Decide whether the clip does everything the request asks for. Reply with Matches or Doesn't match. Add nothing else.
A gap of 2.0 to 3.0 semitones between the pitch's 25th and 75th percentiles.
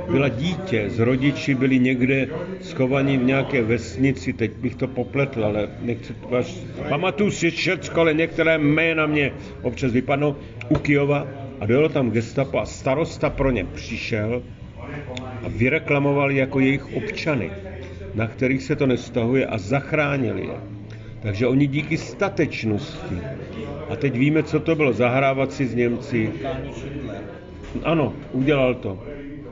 Doesn't match